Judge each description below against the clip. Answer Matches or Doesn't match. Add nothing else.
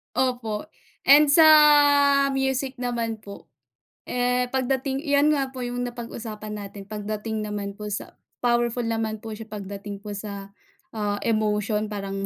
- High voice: Matches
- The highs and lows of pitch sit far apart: Doesn't match